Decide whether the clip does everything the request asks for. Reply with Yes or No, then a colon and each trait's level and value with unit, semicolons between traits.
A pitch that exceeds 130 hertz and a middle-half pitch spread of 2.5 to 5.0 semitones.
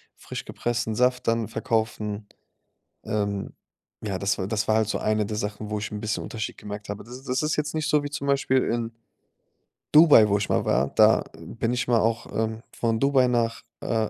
No: low, 115 Hz; average, 2.9 semitones